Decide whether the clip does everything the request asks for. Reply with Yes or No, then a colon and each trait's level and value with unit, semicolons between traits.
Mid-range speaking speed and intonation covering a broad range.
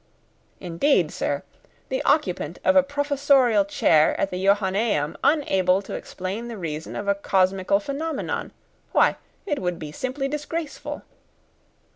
No: slow, 130 wpm; wide, 7.3 semitones